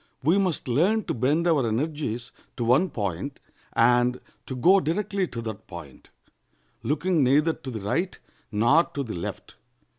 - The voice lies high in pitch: No, low, 135 Hz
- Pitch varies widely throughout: Yes, wide, 6.3 semitones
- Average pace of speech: Yes, average, 155 wpm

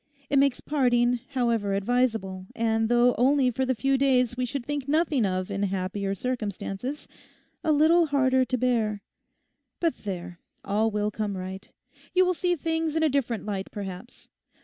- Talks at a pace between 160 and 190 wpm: Yes, average, 165 wpm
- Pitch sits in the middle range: No, high, 245 Hz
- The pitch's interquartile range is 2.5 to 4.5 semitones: No, average, 5.3 semitones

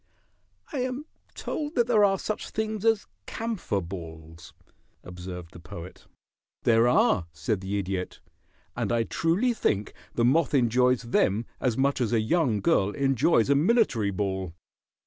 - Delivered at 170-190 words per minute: No, average, 145 wpm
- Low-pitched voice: Yes, low, 120 Hz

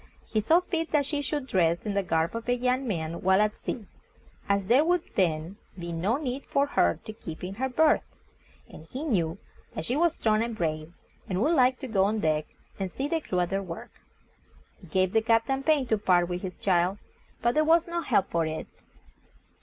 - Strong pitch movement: Yes, wide, 7.1 semitones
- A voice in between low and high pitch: No, high, 210 Hz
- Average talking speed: No, fast, 215 wpm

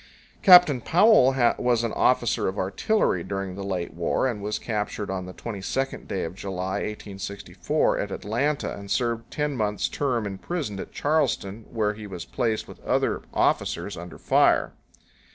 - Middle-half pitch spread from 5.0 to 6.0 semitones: No, average, 4.5 semitones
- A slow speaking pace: No, average, 165 wpm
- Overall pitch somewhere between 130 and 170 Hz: No, low, 105 Hz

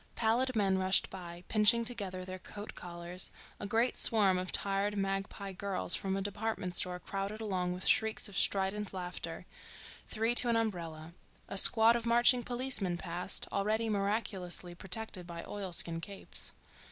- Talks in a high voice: Yes, high, 195 Hz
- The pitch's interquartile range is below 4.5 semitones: Yes, average, 3.3 semitones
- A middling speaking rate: Yes, average, 155 wpm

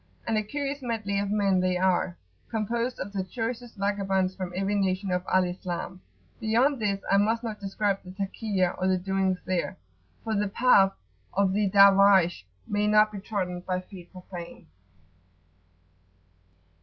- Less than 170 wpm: Yes, average, 155 wpm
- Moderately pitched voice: No, high, 195 Hz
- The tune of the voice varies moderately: No, narrow, 2.3 semitones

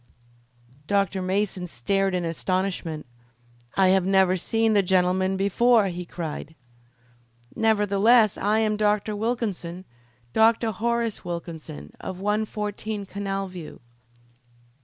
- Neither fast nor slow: No, slow, 105 wpm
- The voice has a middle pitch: No, high, 195 Hz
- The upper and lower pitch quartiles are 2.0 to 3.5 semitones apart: Yes, average, 2.8 semitones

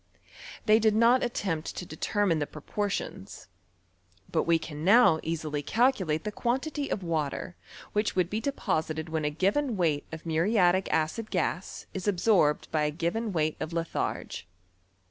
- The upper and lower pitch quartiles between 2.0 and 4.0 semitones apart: No, average, 5.1 semitones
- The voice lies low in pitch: No, medium, 175 Hz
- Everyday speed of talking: Yes, average, 150 wpm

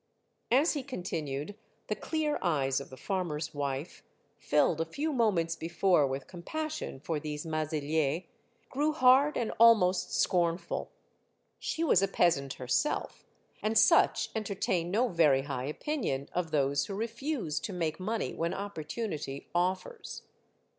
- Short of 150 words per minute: Yes, slow, 135 wpm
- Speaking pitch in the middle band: Yes, medium, 175 Hz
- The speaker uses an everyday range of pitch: No, wide, 7.2 semitones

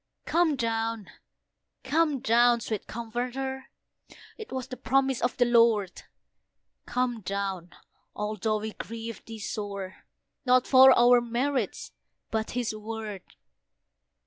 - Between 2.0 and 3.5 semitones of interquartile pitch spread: Yes, average, 2.9 semitones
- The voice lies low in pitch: No, high, 235 Hz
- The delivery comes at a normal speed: No, slow, 115 wpm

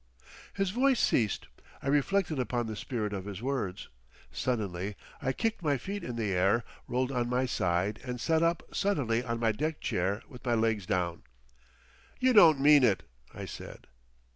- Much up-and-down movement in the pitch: Yes, wide, 6.1 semitones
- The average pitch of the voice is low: Yes, low, 125 Hz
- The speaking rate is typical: Yes, average, 170 wpm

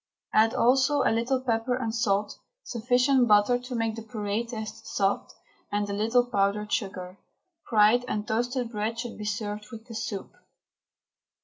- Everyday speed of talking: Yes, average, 155 wpm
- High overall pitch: Yes, high, 225 Hz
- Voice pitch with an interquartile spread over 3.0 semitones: No, average, 2.7 semitones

